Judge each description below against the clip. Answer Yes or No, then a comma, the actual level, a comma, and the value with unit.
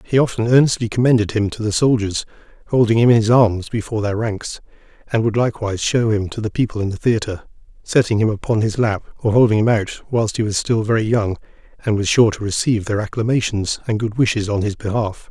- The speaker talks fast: Yes, fast, 215 wpm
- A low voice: Yes, low, 110 Hz